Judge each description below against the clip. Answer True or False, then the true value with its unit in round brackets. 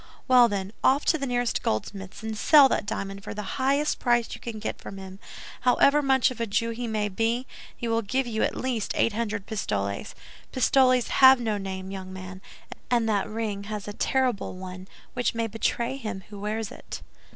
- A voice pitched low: False (225 Hz)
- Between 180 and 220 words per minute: True (195 wpm)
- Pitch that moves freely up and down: False (3.8 semitones)